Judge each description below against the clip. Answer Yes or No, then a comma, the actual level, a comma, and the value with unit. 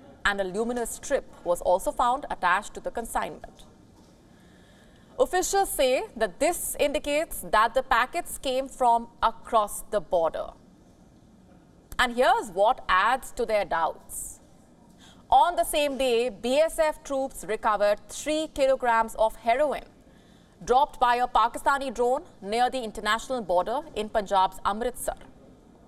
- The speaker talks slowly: Yes, slow, 125 wpm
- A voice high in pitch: Yes, high, 245 Hz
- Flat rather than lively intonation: No, average, 4.8 semitones